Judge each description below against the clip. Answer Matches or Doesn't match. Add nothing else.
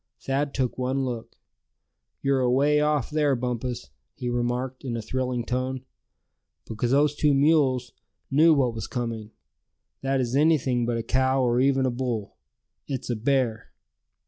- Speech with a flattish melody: Matches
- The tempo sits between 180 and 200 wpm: Doesn't match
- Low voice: Matches